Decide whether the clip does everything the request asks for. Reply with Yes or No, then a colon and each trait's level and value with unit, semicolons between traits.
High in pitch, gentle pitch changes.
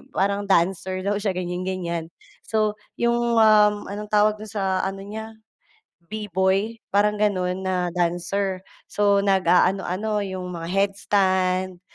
Yes: high, 195 Hz; narrow, 2.2 semitones